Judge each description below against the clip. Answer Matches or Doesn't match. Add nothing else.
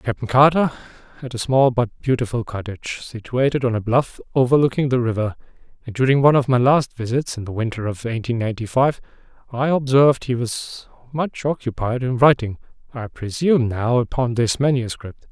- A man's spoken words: Matches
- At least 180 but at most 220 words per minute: Doesn't match